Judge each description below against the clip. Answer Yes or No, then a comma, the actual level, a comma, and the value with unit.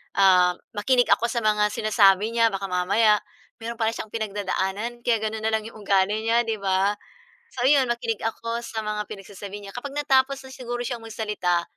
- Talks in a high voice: Yes, high, 220 Hz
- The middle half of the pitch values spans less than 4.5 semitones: Yes, average, 2.8 semitones